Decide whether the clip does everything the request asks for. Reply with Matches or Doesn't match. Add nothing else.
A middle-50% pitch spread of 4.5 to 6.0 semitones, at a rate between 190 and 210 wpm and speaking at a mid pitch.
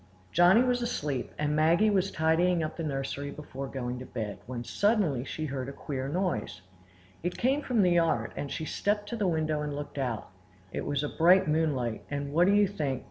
Matches